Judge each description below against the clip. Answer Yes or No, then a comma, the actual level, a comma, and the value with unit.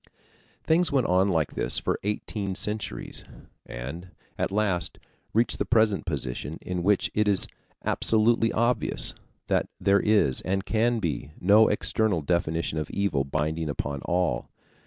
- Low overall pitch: Yes, very low, 95 Hz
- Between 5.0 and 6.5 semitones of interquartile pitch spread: Yes, wide, 5.4 semitones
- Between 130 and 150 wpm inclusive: Yes, average, 140 wpm